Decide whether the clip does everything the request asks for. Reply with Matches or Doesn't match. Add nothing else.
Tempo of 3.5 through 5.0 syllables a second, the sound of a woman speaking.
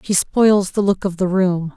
Matches